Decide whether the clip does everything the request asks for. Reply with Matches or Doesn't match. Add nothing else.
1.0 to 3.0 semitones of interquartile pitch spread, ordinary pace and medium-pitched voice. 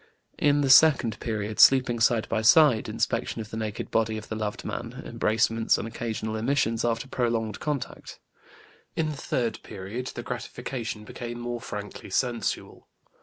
Doesn't match